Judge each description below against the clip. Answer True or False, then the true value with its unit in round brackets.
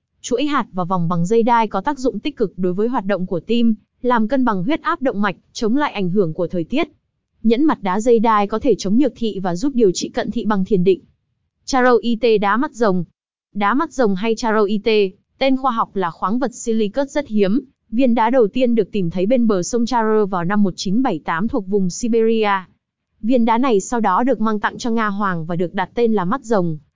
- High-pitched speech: True (220 Hz)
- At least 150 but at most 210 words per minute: False (230 wpm)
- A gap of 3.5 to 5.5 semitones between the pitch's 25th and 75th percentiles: True (3.8 semitones)